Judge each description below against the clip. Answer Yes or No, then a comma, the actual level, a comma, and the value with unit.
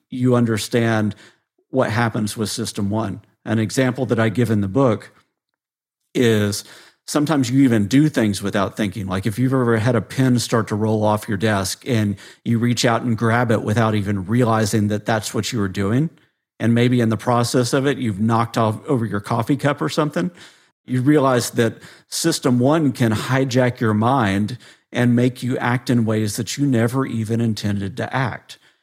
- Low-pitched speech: Yes, low, 115 Hz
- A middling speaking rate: Yes, average, 185 wpm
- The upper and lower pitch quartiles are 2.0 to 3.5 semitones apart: Yes, average, 2.9 semitones